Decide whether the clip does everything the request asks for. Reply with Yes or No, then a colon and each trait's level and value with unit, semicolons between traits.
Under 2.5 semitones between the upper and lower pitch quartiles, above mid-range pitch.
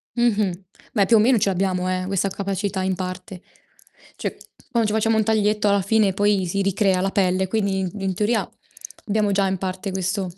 Yes: narrow, 2.1 semitones; high, 195 Hz